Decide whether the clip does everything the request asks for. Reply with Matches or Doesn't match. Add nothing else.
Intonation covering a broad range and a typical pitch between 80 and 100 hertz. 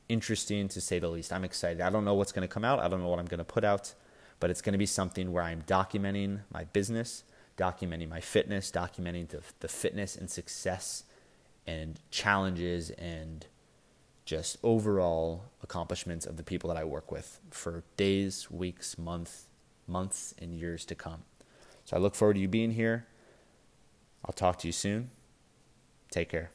Doesn't match